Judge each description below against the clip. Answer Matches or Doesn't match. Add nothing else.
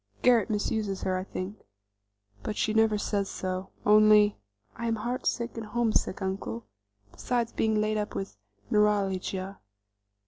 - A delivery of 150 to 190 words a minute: Doesn't match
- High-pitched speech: Matches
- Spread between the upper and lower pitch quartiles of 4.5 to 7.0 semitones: Doesn't match